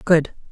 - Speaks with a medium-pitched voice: Yes, medium, 160 Hz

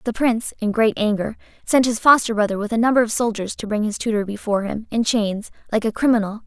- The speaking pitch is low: No, high, 220 Hz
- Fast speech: Yes, fast, 230 wpm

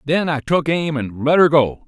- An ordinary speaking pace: No, fast, 255 wpm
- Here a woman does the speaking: No, male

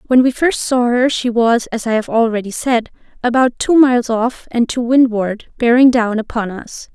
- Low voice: No, high, 240 Hz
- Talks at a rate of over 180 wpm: Yes, average, 200 wpm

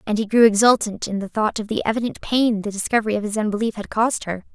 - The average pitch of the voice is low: No, high, 215 Hz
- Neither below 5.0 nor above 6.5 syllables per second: No, 6.7 syllables/s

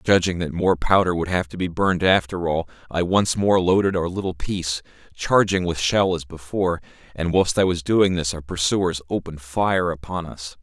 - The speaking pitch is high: No, very low, 90 Hz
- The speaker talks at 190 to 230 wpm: Yes, average, 200 wpm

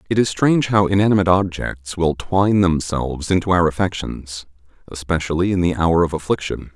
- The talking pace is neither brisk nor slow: Yes, average, 160 wpm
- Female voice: No, male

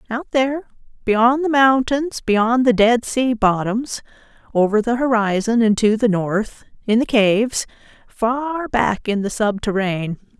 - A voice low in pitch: No, high, 230 Hz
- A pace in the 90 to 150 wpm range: Yes, average, 145 wpm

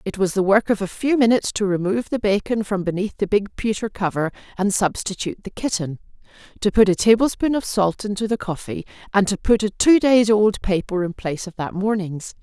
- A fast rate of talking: Yes, fast, 210 wpm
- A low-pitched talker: No, high, 200 Hz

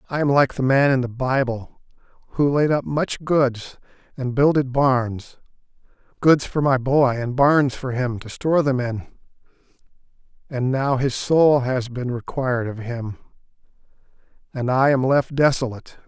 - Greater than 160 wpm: No, average, 155 wpm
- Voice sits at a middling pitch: No, low, 130 Hz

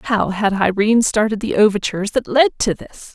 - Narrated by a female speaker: Yes, female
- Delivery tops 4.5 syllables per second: Yes, 5.3 syllables/s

